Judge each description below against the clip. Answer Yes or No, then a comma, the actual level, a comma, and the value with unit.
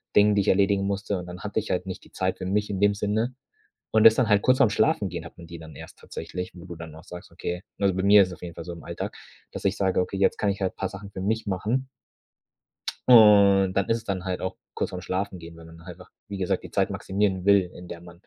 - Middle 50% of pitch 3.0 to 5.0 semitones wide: No, narrow, 2.4 semitones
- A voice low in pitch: Yes, very low, 95 Hz